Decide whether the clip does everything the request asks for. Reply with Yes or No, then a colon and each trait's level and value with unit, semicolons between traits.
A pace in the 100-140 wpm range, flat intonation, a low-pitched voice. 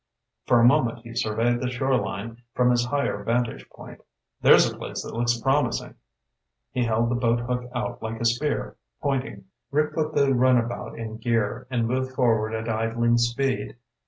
No: average, 170 wpm; narrow, 1.9 semitones; low, 120 Hz